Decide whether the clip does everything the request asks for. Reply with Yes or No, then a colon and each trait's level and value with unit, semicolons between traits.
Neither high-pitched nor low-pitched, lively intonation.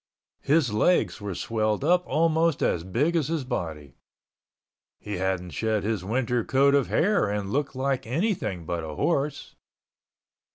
No: low, 120 Hz; wide, 7.5 semitones